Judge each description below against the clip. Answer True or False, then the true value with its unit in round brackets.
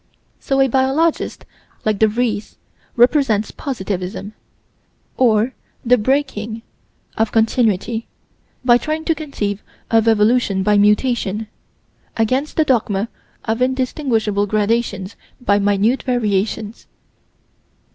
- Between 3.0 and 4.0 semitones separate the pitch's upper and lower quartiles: True (3.6 semitones)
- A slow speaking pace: True (100 wpm)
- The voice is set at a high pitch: True (225 Hz)